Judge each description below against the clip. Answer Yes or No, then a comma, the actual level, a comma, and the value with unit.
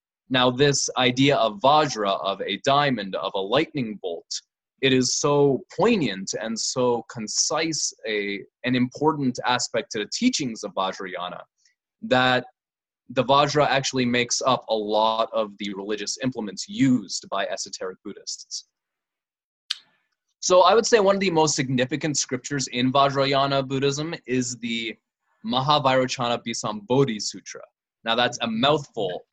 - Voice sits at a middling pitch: No, low, 130 Hz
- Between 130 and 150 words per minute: Yes, slow, 135 wpm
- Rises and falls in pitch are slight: No, average, 3.7 semitones